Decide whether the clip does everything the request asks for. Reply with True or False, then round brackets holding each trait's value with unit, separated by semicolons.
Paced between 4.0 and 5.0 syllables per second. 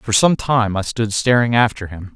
True (4.7 syllables/s)